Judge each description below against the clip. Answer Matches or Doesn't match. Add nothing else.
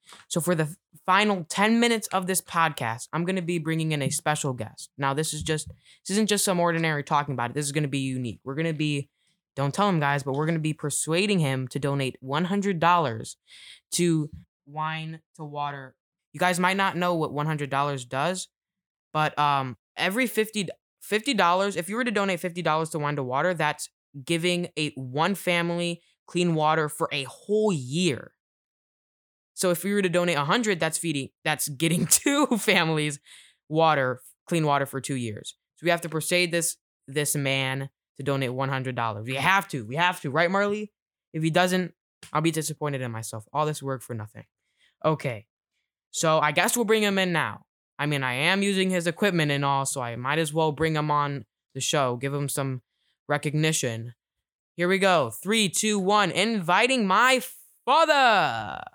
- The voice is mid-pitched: Matches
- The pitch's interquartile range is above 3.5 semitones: Matches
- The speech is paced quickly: Doesn't match